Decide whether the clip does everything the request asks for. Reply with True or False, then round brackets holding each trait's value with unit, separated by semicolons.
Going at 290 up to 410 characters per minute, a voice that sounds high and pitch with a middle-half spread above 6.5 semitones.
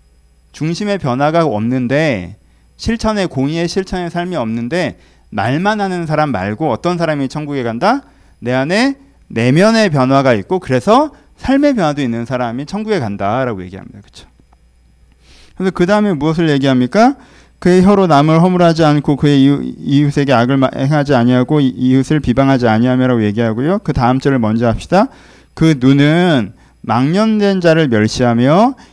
False (335 characters per minute; 140 Hz; 7.0 semitones)